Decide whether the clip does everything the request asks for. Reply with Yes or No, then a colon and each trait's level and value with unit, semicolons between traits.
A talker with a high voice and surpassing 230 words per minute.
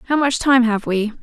Yes: high, 240 Hz; fast, 245 wpm